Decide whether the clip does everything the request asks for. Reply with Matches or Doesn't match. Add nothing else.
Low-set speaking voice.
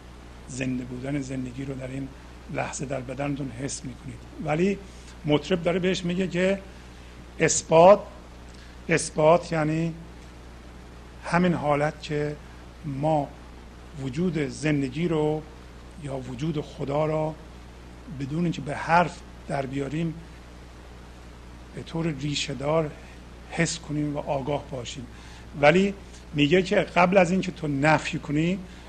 Doesn't match